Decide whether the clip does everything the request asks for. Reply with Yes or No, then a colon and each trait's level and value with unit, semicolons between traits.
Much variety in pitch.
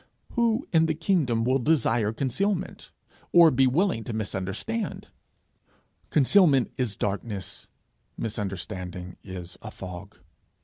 Yes: wide, 8.4 semitones